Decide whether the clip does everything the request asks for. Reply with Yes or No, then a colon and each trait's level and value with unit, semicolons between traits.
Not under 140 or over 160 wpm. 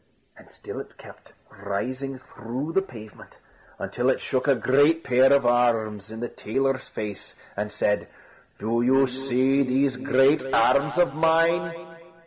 Yes: average, 145 wpm